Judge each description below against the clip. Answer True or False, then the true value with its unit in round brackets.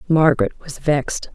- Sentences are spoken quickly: False (135 wpm)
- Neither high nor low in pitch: True (145 Hz)